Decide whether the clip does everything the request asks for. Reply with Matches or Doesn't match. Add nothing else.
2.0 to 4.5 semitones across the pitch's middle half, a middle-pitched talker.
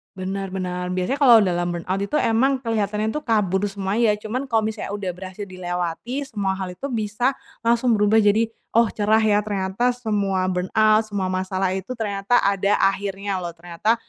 Doesn't match